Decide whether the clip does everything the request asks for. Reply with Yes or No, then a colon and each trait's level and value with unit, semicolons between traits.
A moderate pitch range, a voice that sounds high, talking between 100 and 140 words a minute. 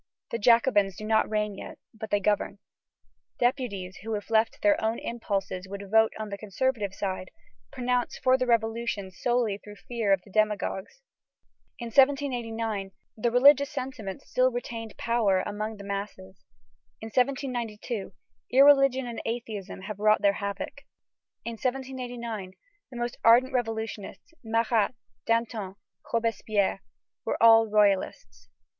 Yes: average, 3.2 semitones; high, 225 Hz; slow, 135 wpm